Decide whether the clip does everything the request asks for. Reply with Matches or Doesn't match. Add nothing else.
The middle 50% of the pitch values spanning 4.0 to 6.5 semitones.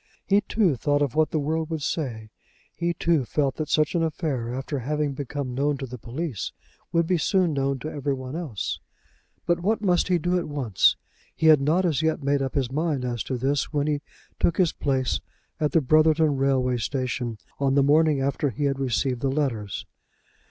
Doesn't match